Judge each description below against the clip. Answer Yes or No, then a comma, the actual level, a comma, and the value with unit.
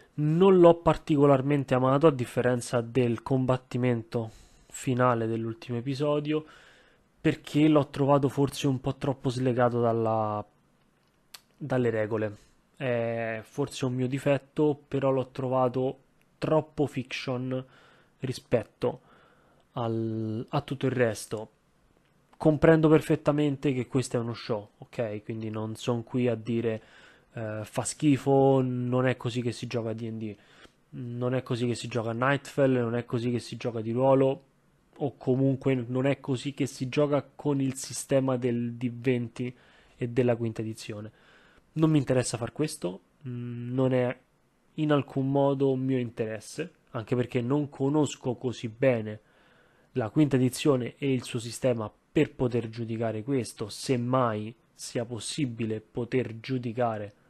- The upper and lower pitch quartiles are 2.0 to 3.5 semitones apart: Yes, average, 2.8 semitones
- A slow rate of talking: No, average, 135 wpm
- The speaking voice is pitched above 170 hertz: No, low, 130 Hz